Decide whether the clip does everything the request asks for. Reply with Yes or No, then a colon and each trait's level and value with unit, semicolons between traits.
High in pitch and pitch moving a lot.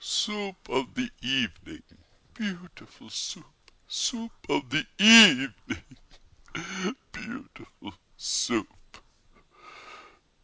Yes: high, 195 Hz; wide, 8.9 semitones